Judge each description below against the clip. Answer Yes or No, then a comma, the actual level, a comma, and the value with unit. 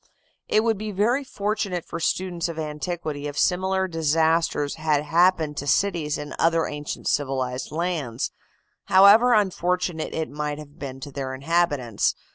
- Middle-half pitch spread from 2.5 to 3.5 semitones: No, average, 4.0 semitones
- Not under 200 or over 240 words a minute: No, average, 145 wpm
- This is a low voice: No, medium, 160 Hz